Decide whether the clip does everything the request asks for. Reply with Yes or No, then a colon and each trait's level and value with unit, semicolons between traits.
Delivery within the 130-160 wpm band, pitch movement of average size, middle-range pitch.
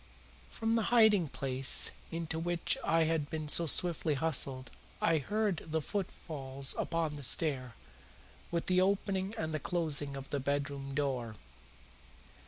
Yes: average, 140 wpm; average, 4.0 semitones; medium, 160 Hz